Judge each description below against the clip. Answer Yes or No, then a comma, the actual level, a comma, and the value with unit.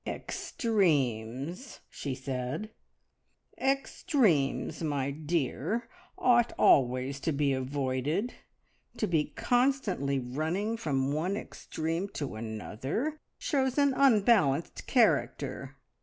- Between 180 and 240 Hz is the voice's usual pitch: No, medium, 155 Hz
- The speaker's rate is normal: No, slow, 90 wpm